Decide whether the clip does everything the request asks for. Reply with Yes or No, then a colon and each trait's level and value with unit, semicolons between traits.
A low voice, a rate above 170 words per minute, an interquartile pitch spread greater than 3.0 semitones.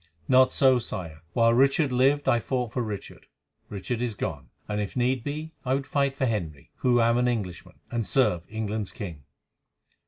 Yes: low, 120 Hz; average, 180 wpm; average, 3.9 semitones